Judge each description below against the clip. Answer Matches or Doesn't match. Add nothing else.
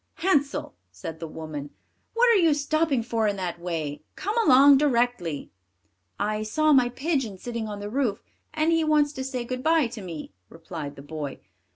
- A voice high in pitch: Matches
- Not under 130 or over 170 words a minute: Doesn't match